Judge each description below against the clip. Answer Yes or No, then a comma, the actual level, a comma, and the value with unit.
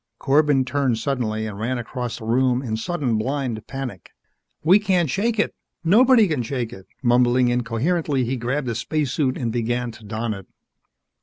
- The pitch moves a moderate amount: Yes, average, 4.0 semitones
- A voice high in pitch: No, low, 125 Hz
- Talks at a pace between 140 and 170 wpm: Yes, average, 165 wpm